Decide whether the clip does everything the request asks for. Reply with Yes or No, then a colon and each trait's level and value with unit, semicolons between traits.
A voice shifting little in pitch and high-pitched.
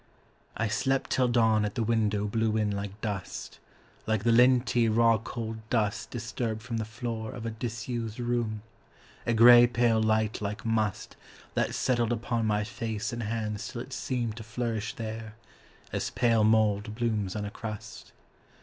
No: narrow, 1.7 semitones; low, 110 Hz